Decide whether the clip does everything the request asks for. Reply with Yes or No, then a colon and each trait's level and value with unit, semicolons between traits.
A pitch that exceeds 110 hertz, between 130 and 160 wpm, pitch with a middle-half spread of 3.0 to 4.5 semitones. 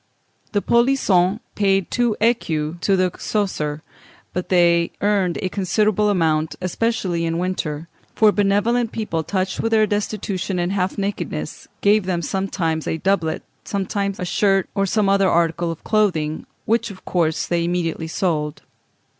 Yes: high, 190 Hz; average, 145 wpm; average, 3.3 semitones